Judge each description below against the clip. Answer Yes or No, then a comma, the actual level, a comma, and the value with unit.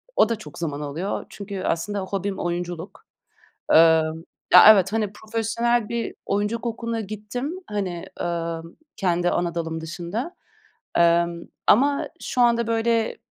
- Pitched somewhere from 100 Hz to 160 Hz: No, high, 200 Hz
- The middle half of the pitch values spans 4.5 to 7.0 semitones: Yes, average, 4.9 semitones